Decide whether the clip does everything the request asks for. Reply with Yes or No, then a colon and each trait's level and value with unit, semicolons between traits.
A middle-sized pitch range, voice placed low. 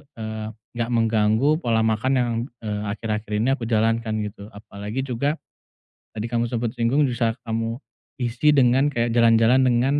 No: narrow, 1.8 semitones; low, 115 Hz